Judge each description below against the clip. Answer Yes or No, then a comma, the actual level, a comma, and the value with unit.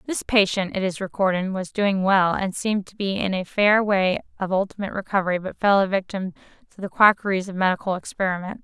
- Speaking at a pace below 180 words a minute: No, average, 200 wpm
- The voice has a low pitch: No, high, 195 Hz